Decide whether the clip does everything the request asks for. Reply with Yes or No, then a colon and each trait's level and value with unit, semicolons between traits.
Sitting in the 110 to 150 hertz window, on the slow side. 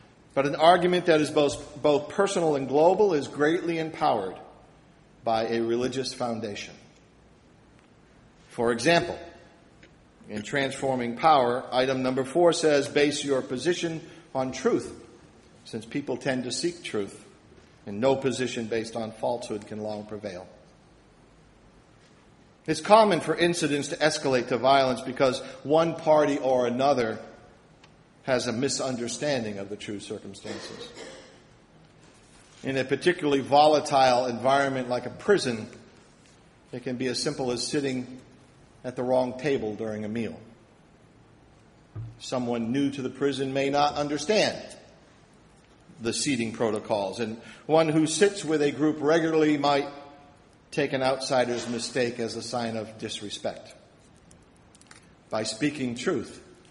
Yes: low, 135 Hz; slow, 125 wpm